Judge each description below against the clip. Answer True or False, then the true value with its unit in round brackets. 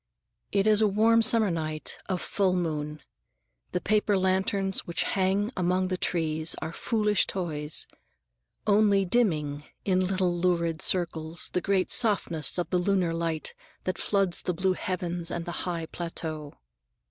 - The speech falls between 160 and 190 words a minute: False (145 wpm)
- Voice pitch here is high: False (180 Hz)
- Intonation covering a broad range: False (3.0 semitones)